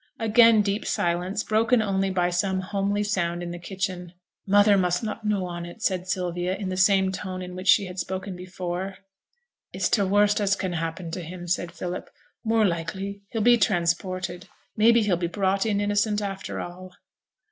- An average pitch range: No, narrow, 2.3 semitones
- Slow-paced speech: No, average, 180 wpm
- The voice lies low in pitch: No, high, 190 Hz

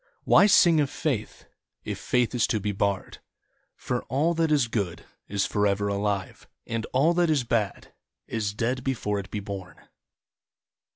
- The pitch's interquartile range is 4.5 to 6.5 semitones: Yes, average, 5.0 semitones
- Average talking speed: Yes, average, 160 wpm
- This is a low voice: Yes, low, 115 Hz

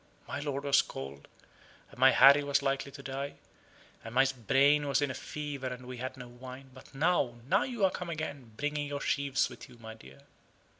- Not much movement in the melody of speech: Yes, narrow, 2.2 semitones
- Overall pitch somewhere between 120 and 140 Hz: Yes, low, 135 Hz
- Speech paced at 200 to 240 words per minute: Yes, fast, 205 wpm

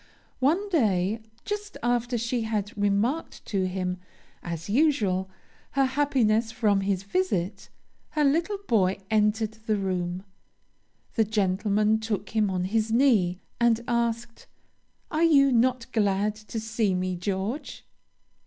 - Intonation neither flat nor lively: Yes, average, 3.8 semitones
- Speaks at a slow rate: Yes, slow, 125 wpm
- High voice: Yes, high, 220 Hz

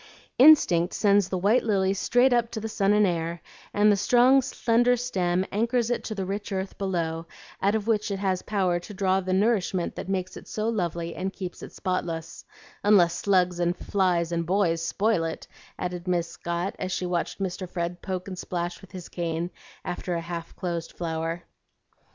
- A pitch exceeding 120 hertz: Yes, medium, 185 Hz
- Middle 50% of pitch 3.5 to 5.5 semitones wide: No, average, 3.0 semitones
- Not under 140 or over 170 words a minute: No, average, 190 wpm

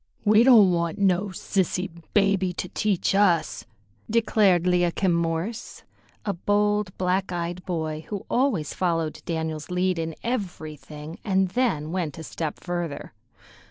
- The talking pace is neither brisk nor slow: No, slow, 130 wpm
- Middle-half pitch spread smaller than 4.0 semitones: Yes, average, 3.4 semitones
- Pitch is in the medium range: Yes, medium, 180 Hz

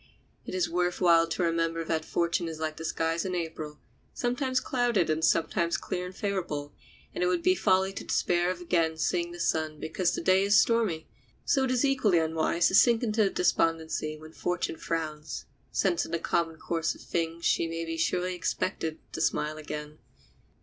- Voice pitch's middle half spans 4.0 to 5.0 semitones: No, narrow, 2.4 semitones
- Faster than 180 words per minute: Yes, average, 190 wpm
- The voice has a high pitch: No, medium, 170 Hz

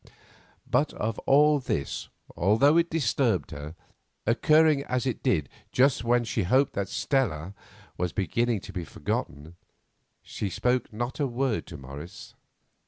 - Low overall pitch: Yes, low, 115 Hz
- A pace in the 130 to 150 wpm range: Yes, average, 140 wpm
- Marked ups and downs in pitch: Yes, wide, 7.0 semitones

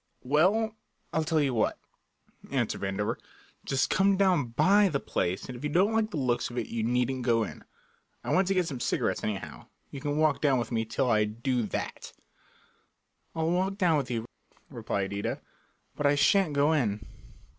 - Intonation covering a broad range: Yes, wide, 6.9 semitones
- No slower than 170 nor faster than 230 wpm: Yes, average, 190 wpm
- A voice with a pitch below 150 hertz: Yes, medium, 140 Hz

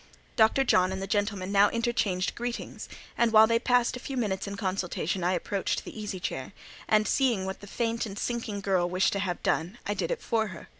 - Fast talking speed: Yes, fast, 215 wpm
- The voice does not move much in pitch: No, average, 3.5 semitones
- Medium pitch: No, high, 205 Hz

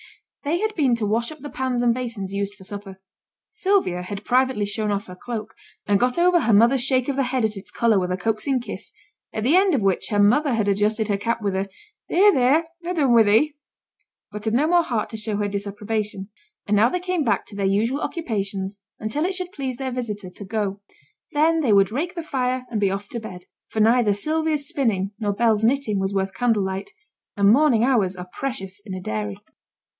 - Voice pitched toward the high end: Yes, high, 225 Hz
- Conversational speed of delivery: No, fast, 220 wpm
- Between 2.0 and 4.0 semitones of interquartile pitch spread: No, average, 4.9 semitones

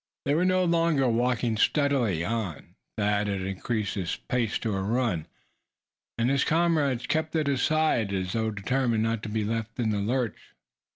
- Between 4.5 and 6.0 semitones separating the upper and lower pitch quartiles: Yes, average, 5.0 semitones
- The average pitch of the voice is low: Yes, low, 115 Hz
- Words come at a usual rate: Yes, average, 175 wpm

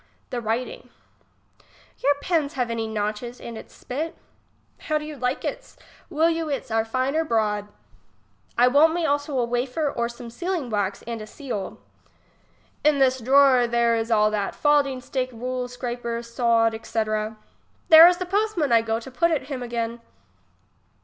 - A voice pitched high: Yes, very high, 250 Hz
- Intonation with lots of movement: No, average, 4.1 semitones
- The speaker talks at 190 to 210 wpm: No, average, 170 wpm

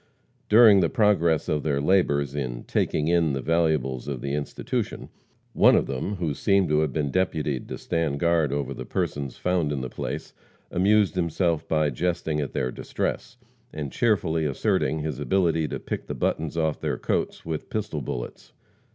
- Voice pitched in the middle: No, very low, 80 Hz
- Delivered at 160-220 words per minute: Yes, average, 175 wpm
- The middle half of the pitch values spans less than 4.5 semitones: Yes, average, 3.3 semitones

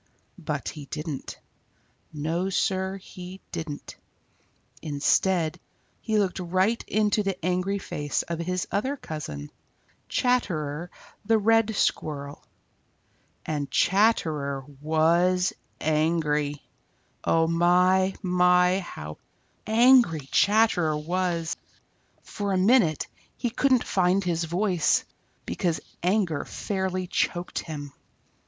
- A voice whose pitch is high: No, medium, 180 Hz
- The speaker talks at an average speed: No, slow, 100 wpm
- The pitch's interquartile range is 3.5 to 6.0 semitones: Yes, average, 3.8 semitones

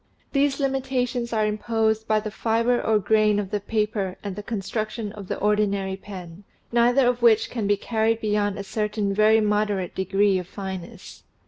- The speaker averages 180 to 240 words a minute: Yes, average, 185 wpm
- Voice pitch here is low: No, high, 215 Hz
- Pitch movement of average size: No, narrow, 2.1 semitones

